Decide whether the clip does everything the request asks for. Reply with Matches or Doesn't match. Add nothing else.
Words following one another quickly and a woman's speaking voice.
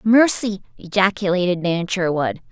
Doesn't match